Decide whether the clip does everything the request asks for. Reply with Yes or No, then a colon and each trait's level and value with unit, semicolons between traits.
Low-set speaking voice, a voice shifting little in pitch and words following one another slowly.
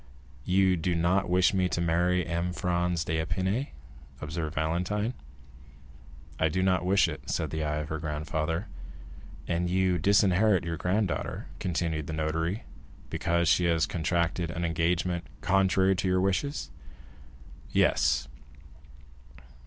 Yes: very low, 85 Hz; narrow, 2.3 semitones; slow, 130 wpm